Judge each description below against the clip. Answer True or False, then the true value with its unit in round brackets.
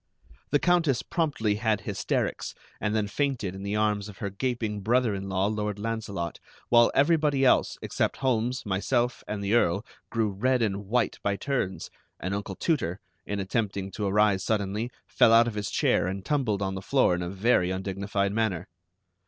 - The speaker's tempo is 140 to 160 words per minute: False (175 wpm)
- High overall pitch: False (105 Hz)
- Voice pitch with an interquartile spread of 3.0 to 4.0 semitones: True (3.4 semitones)